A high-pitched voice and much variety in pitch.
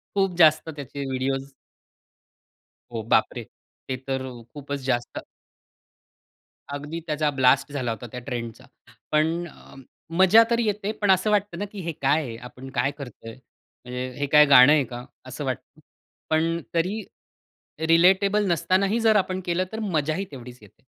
No: medium, 150 Hz; wide, 6.2 semitones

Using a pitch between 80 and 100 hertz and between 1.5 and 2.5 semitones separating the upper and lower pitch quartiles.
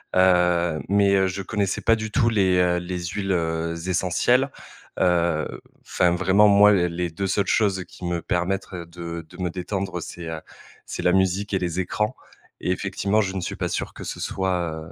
Yes: very low, 90 Hz; narrow, 2.1 semitones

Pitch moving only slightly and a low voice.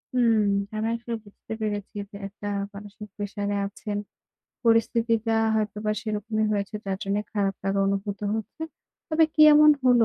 No: narrow, 2.0 semitones; high, 210 Hz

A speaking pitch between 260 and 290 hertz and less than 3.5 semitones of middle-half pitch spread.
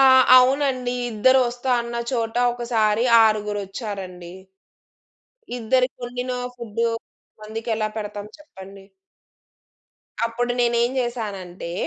No: high, 230 Hz; average, 3.0 semitones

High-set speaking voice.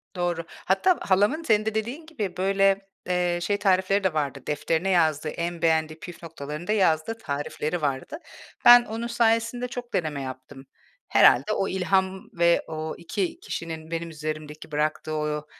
No: medium, 175 Hz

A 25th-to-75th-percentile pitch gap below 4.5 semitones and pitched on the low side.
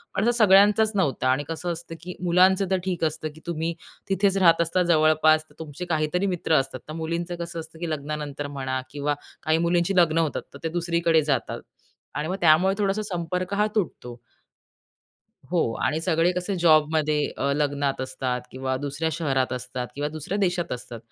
No: average, 3.4 semitones; medium, 160 Hz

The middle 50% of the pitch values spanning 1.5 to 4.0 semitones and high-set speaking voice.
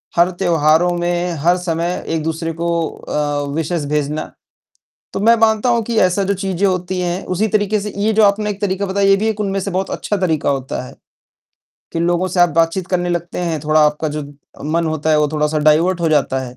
No: average, 3.7 semitones; medium, 175 Hz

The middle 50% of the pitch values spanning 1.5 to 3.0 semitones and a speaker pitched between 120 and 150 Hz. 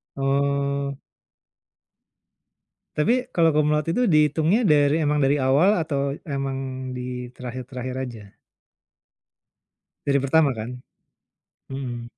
Yes: narrow, 2.6 semitones; medium, 140 Hz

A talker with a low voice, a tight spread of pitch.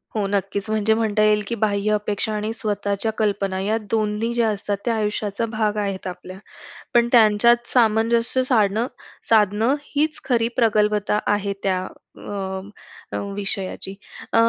No: high, 215 Hz; narrow, 1.9 semitones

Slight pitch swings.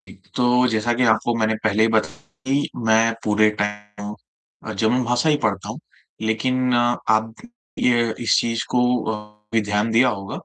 Yes: narrow, 2.2 semitones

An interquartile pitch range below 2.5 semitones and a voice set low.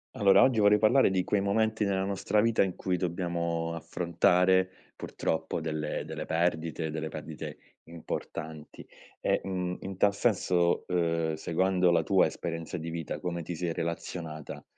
No: average, 2.8 semitones; very low, 85 Hz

